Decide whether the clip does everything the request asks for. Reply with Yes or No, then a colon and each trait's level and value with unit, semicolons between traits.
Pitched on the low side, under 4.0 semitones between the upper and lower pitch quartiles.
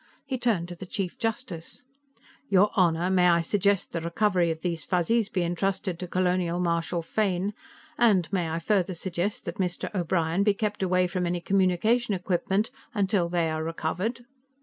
No: medium, 180 Hz; average, 2.9 semitones